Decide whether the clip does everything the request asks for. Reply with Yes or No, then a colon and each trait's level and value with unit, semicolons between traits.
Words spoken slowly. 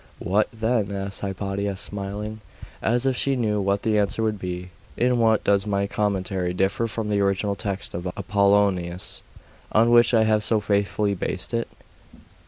No: average, 165 wpm